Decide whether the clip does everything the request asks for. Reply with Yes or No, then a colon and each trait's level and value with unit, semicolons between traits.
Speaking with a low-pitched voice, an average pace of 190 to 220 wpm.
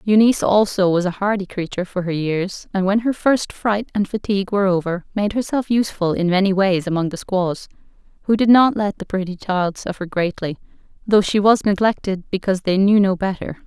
No: high, 195 Hz; average, 200 wpm